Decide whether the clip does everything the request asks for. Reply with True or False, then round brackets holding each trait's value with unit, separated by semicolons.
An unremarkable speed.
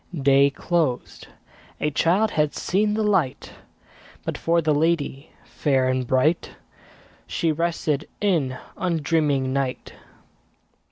False (110 wpm)